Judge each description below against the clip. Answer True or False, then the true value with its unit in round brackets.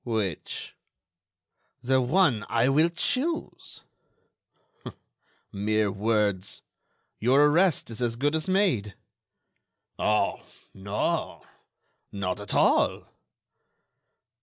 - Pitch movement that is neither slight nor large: False (6.5 semitones)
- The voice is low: True (115 Hz)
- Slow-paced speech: True (80 wpm)